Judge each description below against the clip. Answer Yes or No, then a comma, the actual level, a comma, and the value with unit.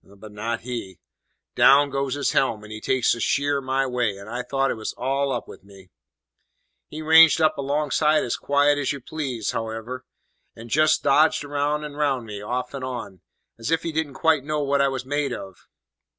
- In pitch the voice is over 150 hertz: No, low, 135 Hz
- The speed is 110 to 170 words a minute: No, average, 200 wpm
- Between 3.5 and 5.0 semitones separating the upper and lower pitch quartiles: Yes, average, 4.1 semitones